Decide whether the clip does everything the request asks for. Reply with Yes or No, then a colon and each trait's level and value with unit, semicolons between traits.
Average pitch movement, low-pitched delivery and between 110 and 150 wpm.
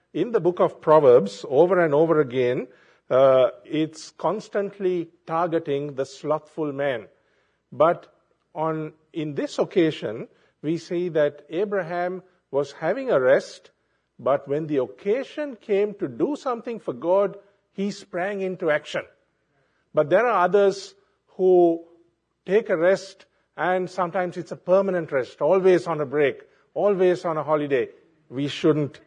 No: average, 4.3 semitones; medium, 175 Hz; average, 140 wpm